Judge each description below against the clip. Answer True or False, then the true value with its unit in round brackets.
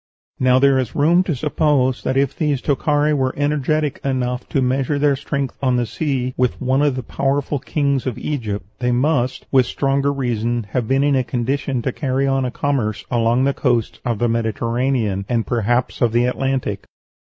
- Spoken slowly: False (190 wpm)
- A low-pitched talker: True (130 Hz)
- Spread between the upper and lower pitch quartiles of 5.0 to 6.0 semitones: False (2.5 semitones)